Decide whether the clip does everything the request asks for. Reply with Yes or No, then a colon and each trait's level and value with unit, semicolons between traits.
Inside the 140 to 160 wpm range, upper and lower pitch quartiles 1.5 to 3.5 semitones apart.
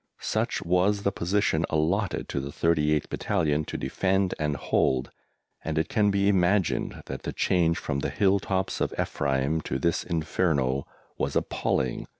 No: average, 155 wpm; average, 4.5 semitones